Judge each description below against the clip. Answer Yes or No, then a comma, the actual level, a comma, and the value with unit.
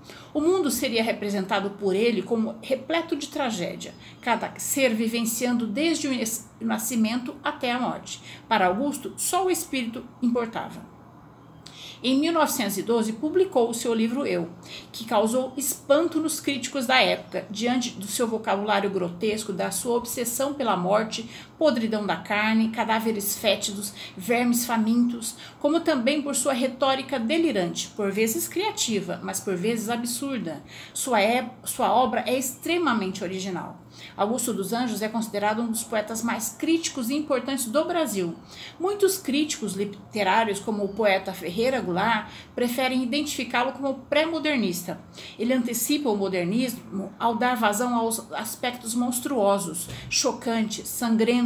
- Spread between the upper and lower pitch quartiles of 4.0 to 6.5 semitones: Yes, average, 4.3 semitones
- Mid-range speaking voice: No, high, 235 Hz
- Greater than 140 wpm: No, average, 135 wpm